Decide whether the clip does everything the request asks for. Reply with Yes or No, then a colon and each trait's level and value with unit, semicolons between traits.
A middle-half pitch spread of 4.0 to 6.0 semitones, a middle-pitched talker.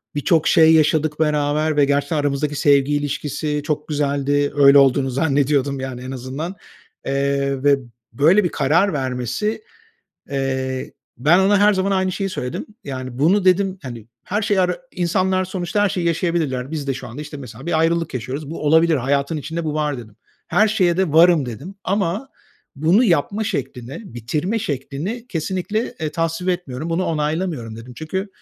Yes: average, 4.5 semitones; medium, 150 Hz